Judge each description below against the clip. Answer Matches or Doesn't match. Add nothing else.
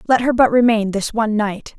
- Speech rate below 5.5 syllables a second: Doesn't match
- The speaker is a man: Doesn't match